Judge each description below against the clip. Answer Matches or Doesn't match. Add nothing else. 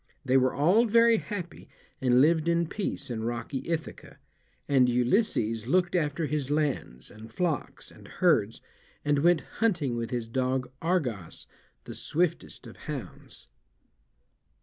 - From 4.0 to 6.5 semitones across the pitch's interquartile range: Matches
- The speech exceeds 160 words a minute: Doesn't match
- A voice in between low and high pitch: Matches